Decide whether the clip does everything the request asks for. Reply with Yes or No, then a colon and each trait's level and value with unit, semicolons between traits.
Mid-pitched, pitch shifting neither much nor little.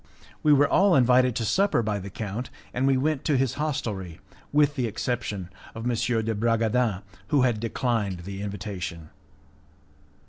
No: low, 115 Hz; average, 4.4 semitones